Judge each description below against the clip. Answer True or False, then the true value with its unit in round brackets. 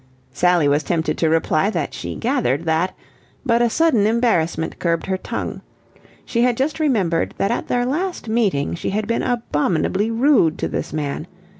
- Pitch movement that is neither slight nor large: False (6.7 semitones)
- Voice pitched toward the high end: True (205 Hz)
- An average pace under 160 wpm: False (170 wpm)